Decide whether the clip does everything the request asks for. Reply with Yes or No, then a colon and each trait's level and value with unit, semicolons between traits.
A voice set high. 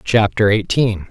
No: low, 105 Hz